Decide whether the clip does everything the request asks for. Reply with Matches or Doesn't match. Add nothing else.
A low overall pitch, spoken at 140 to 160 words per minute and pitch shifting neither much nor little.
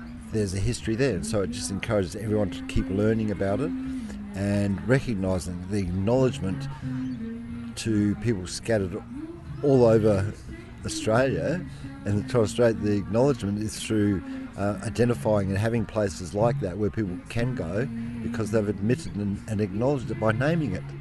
Matches